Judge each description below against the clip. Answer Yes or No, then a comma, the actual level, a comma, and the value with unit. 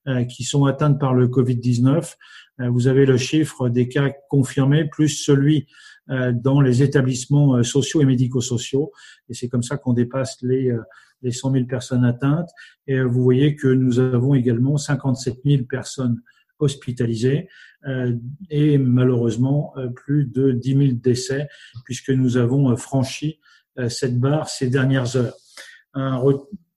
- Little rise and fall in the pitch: Yes, narrow, 2.0 semitones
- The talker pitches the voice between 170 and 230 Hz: No, low, 130 Hz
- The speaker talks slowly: Yes, slow, 135 wpm